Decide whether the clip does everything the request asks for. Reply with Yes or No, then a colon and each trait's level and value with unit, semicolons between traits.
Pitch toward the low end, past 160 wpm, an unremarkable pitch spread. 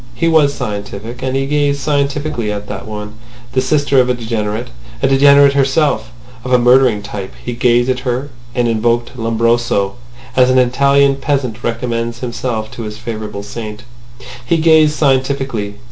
No: low, 125 Hz; average, 155 wpm; average, 3.6 semitones